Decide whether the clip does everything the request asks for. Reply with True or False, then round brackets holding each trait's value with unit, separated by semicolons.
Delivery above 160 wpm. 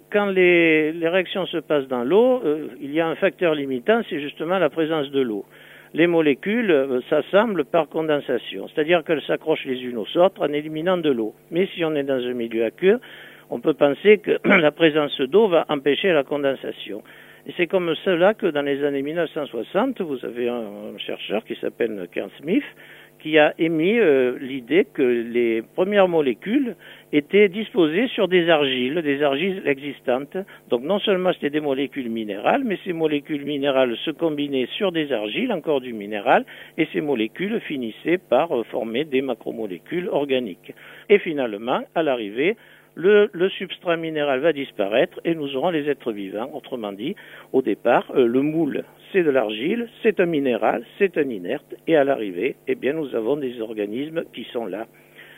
True (180 wpm)